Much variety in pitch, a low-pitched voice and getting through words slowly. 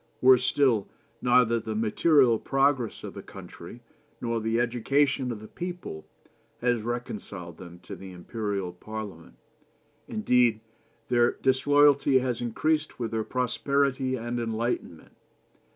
No: average, 3.3 semitones; low, 120 Hz; slow, 120 wpm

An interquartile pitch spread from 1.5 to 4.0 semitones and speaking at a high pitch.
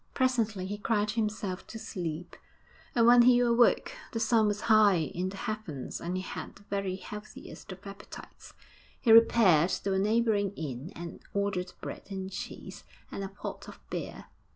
Yes: average, 3.2 semitones; high, 200 Hz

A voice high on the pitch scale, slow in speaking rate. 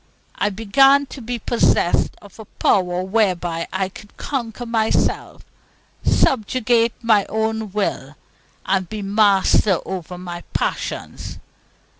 Yes: high, 210 Hz; slow, 115 wpm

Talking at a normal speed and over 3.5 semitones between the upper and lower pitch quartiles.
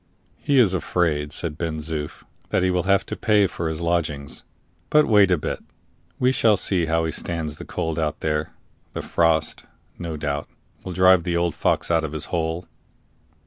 No: average, 185 wpm; average, 2.8 semitones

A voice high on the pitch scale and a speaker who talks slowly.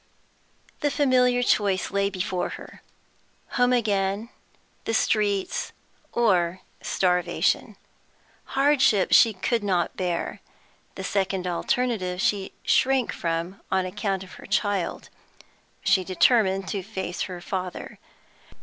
Yes: high, 195 Hz; slow, 110 wpm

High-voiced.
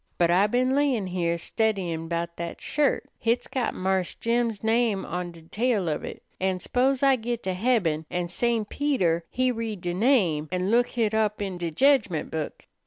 Yes: high, 205 Hz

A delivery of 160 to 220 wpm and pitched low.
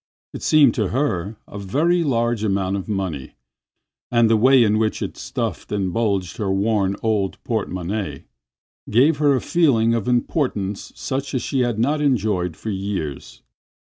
Yes: average, 165 wpm; low, 110 Hz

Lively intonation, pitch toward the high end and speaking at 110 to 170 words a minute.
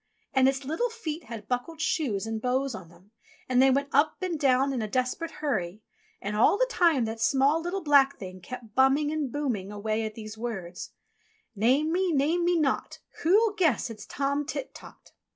No: wide, 5.9 semitones; very high, 270 Hz; average, 190 wpm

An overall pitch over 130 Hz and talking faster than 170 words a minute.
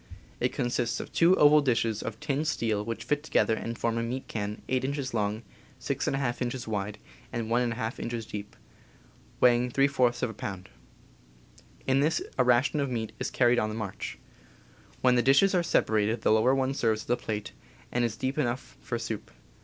No: low, 120 Hz; average, 185 wpm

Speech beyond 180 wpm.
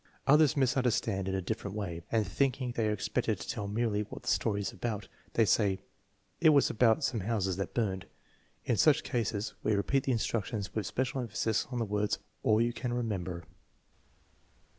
Yes: average, 190 wpm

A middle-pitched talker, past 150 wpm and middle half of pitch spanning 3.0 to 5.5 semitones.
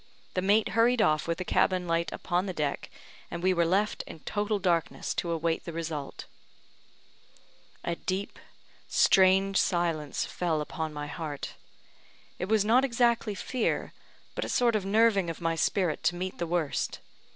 Yes: medium, 180 Hz; average, 165 wpm; average, 3.5 semitones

